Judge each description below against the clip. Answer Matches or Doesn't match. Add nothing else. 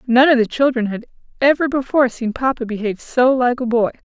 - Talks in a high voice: Matches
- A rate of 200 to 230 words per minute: Matches